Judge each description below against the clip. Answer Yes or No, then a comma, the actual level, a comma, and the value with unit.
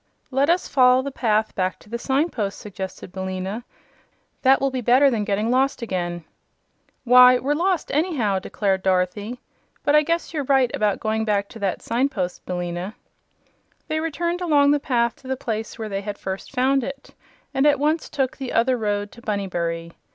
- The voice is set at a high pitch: Yes, high, 235 Hz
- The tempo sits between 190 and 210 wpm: No, average, 180 wpm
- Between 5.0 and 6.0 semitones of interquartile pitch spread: Yes, wide, 5.4 semitones